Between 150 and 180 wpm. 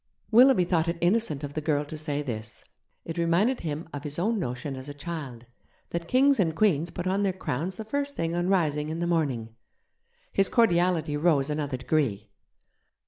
No: average, 190 wpm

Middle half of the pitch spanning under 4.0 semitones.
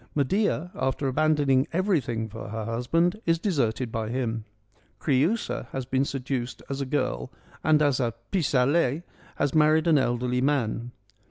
No: average, 4.3 semitones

